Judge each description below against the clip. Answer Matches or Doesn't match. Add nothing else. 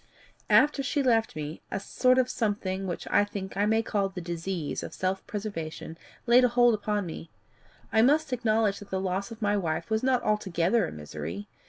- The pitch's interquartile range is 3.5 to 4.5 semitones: Matches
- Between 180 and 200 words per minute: Matches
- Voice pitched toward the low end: Doesn't match